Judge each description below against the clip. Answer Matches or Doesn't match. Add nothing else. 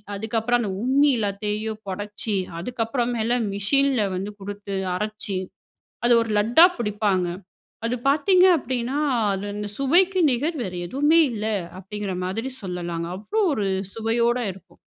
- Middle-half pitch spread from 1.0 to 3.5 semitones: Doesn't match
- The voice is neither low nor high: Doesn't match